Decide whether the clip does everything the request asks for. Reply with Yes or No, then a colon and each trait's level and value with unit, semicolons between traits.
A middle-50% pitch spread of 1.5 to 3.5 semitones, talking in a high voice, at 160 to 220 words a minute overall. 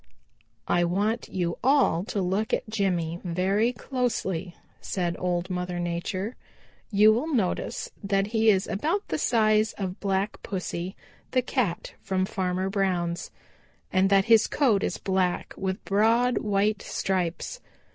No: average, 3.2 semitones; high, 195 Hz; slow, 135 wpm